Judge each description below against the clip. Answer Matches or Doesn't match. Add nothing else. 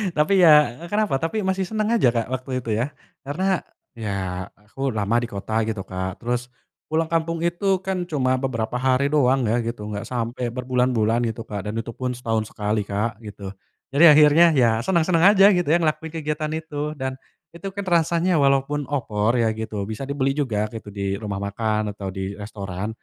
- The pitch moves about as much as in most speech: Doesn't match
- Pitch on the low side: Matches